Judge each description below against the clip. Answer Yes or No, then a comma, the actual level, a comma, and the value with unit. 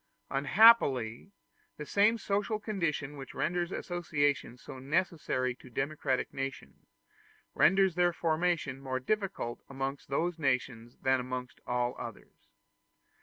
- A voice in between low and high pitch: Yes, medium, 145 Hz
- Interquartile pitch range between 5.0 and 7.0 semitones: Yes, wide, 5.4 semitones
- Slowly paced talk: Yes, slow, 115 wpm